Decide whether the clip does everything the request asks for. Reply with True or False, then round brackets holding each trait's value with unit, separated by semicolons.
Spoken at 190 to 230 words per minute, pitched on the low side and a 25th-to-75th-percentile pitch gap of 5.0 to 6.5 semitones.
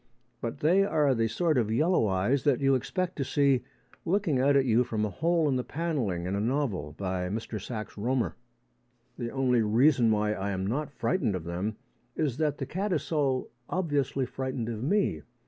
True (195 wpm; 130 Hz; 5.6 semitones)